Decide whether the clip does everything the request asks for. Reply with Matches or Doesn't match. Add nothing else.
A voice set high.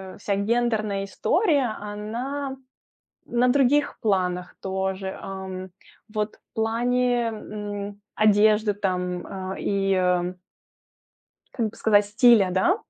Matches